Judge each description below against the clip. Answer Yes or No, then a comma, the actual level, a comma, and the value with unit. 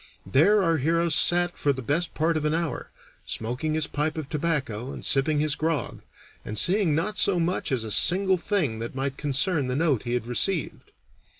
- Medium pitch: Yes, medium, 155 Hz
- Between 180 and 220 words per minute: Yes, average, 195 wpm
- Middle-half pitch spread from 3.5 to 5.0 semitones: Yes, average, 4.1 semitones